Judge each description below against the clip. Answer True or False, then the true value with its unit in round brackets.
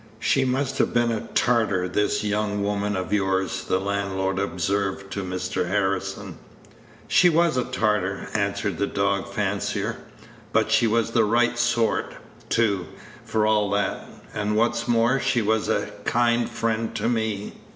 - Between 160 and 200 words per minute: False (150 wpm)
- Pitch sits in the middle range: False (105 Hz)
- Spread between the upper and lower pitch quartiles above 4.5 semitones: False (2.9 semitones)